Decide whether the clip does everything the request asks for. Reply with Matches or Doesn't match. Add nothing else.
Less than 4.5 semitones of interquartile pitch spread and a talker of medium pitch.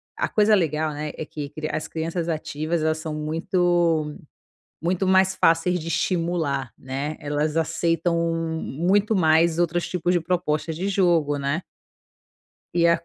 Matches